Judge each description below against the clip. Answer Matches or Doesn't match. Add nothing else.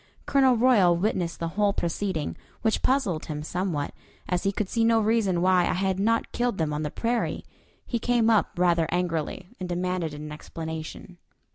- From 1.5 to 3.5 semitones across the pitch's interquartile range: Doesn't match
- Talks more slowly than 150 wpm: Doesn't match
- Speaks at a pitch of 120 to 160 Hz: Doesn't match